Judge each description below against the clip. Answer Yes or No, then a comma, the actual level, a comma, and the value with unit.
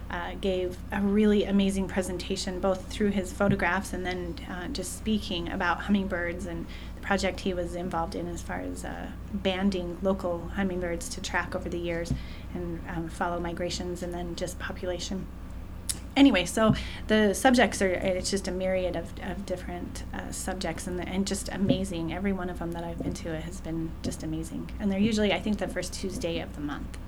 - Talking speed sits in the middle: Yes, average, 195 wpm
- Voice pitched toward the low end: No, medium, 180 Hz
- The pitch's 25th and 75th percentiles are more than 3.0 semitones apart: No, average, 2.7 semitones